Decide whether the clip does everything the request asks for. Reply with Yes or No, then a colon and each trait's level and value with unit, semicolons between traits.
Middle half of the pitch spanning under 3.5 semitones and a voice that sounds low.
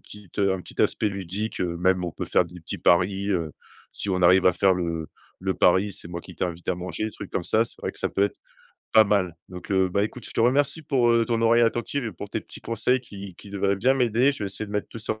No: average, 3.8 semitones; low, 100 Hz